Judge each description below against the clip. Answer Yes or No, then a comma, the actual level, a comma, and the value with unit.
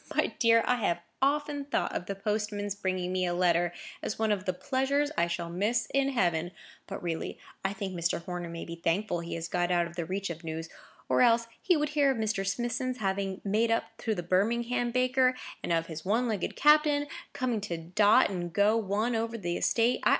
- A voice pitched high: Yes, high, 205 Hz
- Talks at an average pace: No, fast, 210 wpm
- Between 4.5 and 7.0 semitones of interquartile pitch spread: Yes, average, 5.3 semitones